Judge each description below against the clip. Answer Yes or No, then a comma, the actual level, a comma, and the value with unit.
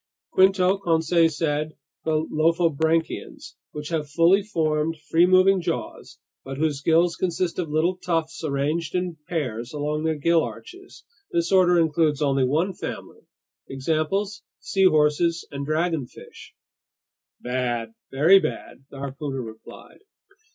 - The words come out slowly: Yes, slow, 125 wpm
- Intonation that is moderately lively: Yes, average, 3.1 semitones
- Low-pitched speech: No, medium, 160 Hz